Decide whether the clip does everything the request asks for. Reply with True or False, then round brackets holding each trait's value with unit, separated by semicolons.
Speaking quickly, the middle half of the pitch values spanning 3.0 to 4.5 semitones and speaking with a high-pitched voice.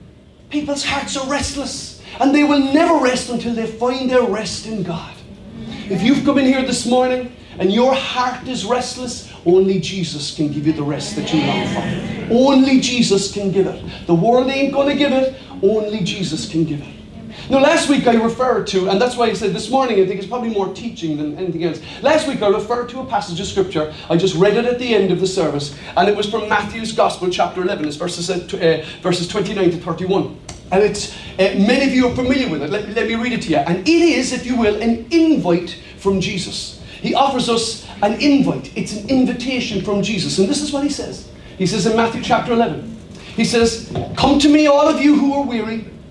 False (225 wpm; 5.2 semitones; 225 Hz)